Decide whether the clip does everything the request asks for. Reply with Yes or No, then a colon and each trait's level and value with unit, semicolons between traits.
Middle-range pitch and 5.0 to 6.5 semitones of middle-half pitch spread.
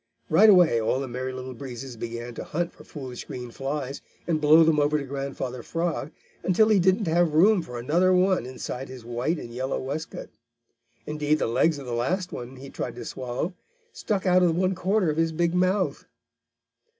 Yes: medium, 150 Hz; wide, 5.5 semitones